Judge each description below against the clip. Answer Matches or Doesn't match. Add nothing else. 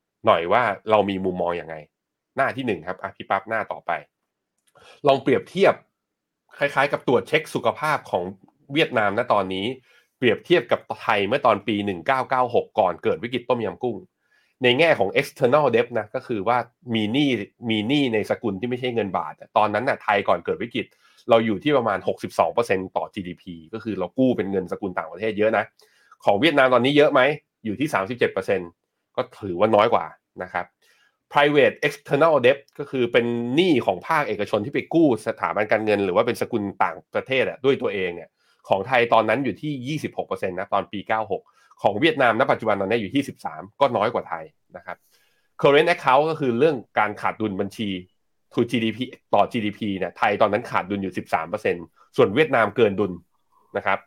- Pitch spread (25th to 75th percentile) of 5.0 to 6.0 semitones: Doesn't match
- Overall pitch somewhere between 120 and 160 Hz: Doesn't match